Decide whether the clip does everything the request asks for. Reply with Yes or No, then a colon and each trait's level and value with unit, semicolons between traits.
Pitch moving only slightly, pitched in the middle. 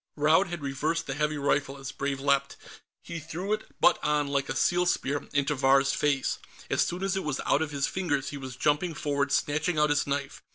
Yes: narrow, 2.3 semitones; medium, 145 Hz